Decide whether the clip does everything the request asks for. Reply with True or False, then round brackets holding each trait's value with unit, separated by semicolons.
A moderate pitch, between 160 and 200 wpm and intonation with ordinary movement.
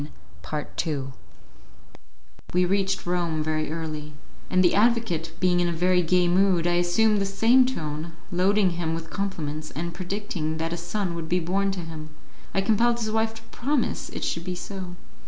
True (175 Hz; 175 wpm; 3.4 semitones)